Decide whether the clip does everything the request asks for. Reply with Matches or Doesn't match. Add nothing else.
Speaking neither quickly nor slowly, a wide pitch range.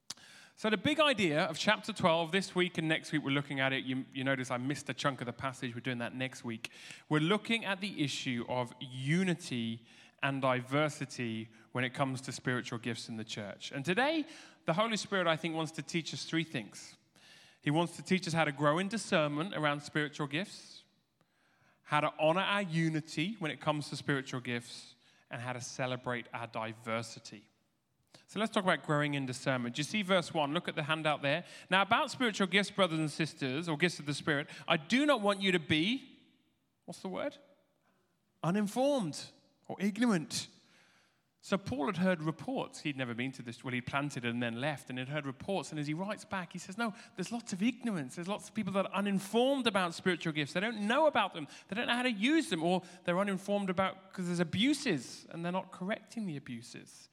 Doesn't match